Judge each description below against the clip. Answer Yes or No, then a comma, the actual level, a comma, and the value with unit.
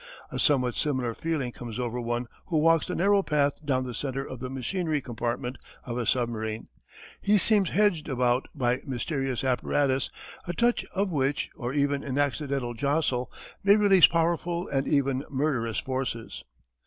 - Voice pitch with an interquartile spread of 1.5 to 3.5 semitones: No, average, 4.3 semitones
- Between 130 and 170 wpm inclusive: Yes, average, 160 wpm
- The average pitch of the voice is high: No, low, 135 Hz